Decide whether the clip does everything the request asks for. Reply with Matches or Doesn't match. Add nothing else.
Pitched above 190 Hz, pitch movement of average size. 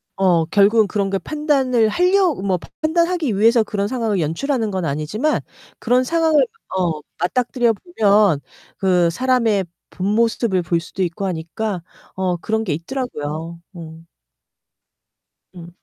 Doesn't match